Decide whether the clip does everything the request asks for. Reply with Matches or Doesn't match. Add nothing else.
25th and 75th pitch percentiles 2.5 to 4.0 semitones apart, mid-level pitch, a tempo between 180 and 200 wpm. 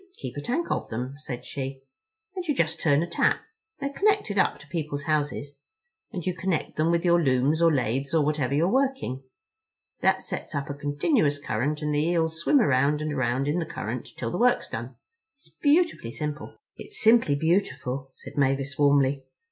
Doesn't match